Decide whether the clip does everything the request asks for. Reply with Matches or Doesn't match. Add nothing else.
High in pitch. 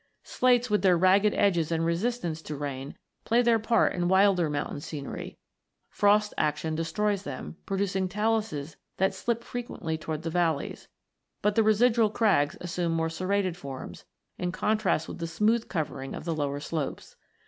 Doesn't match